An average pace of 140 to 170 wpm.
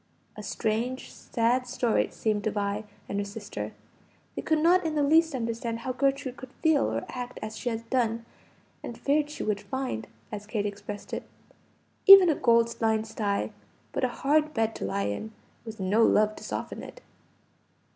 No: average, 185 wpm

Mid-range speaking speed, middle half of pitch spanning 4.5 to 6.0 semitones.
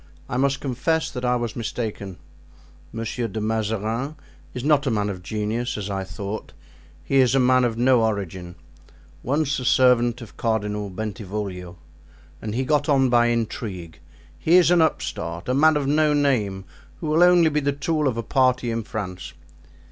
Yes: average, 170 wpm; average, 4.8 semitones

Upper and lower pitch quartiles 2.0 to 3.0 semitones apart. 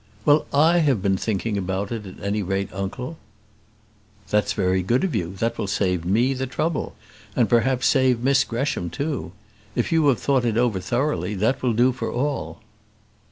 No: average, 5.3 semitones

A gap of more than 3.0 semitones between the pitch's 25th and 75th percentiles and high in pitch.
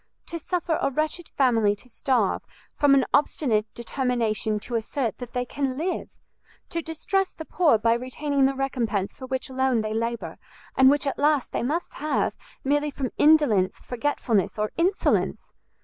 Yes: average, 4.3 semitones; very high, 265 Hz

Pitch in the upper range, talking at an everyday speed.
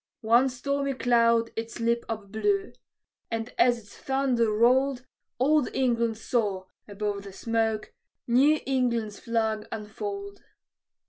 No: high, 235 Hz; slow, 115 wpm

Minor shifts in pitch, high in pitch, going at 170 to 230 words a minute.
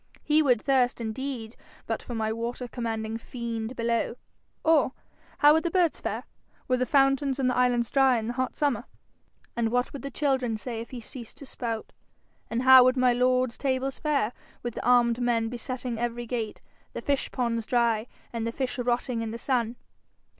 Yes: narrow, 2.2 semitones; high, 245 Hz; average, 190 wpm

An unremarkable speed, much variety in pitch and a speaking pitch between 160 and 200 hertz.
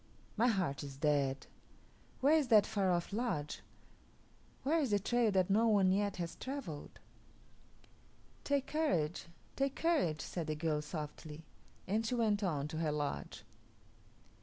Yes: average, 145 wpm; wide, 7.4 semitones; high, 190 Hz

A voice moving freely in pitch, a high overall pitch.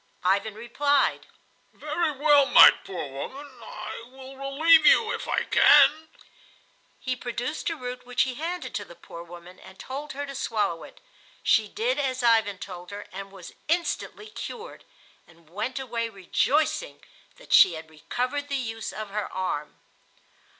Yes: wide, 6.5 semitones; high, 245 Hz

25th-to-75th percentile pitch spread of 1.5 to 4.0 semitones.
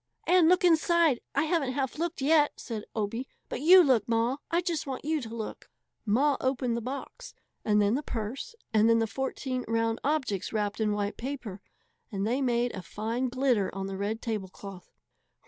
No: average, 4.8 semitones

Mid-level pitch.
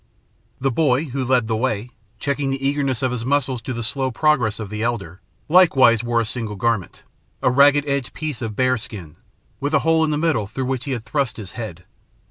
No: low, 125 Hz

